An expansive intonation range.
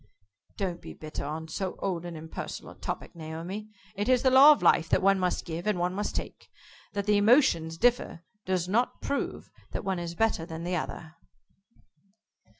No: average, 4.2 semitones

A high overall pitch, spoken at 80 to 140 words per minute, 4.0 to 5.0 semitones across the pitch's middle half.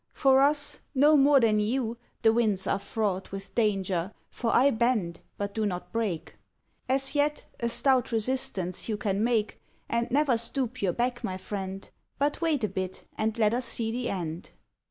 No: high, 225 Hz; average, 175 wpm; average, 4.6 semitones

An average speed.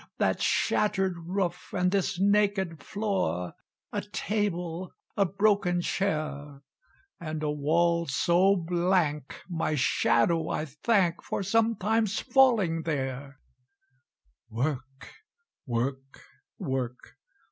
No: slow, 95 wpm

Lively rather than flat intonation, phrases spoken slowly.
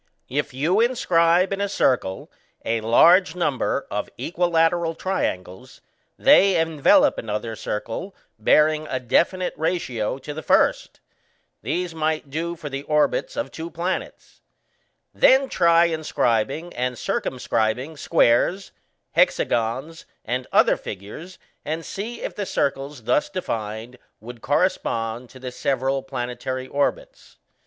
Yes: wide, 5.9 semitones; slow, 130 wpm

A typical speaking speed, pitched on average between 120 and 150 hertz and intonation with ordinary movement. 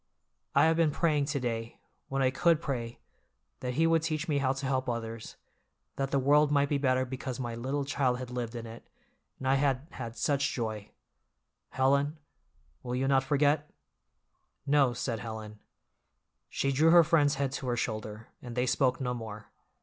Yes: average, 180 wpm; low, 135 Hz; average, 3.1 semitones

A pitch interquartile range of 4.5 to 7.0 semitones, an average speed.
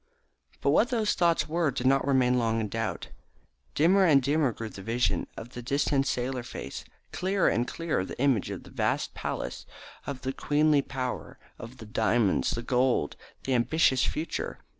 No: average, 4.1 semitones; average, 175 wpm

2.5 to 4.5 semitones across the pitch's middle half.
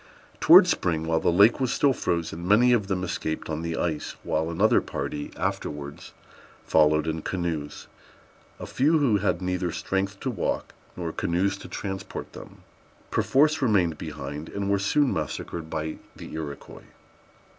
Yes: average, 4.2 semitones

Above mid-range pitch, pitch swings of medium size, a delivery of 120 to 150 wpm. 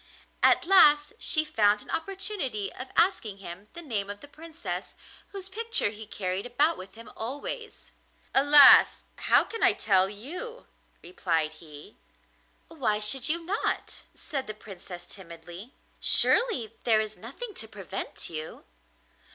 No: high, 230 Hz; wide, 8.7 semitones; average, 140 wpm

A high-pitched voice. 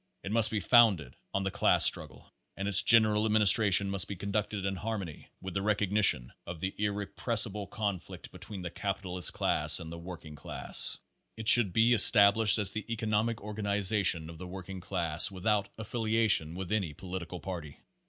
No: low, 100 Hz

